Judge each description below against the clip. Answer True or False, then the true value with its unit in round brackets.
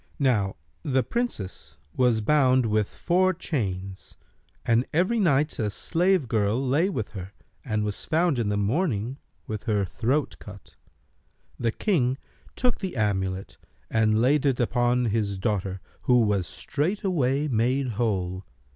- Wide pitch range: True (6.0 semitones)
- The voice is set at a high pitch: False (120 Hz)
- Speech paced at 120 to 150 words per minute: True (140 wpm)